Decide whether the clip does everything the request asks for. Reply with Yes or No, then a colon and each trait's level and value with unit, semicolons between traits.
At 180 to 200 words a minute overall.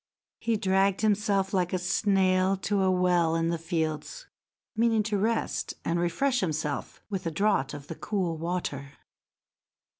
No: average, 150 wpm